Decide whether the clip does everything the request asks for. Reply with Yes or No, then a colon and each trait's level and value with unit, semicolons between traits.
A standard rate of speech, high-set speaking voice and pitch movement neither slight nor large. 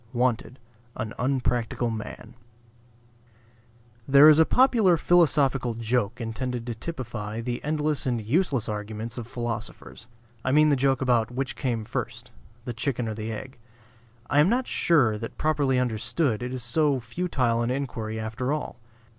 No: average, 150 wpm; low, 125 Hz; average, 3.7 semitones